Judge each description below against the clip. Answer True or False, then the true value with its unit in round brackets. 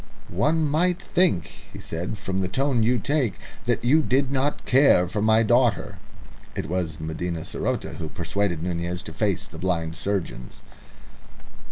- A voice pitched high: False (100 Hz)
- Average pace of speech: True (155 wpm)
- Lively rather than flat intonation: True (7.1 semitones)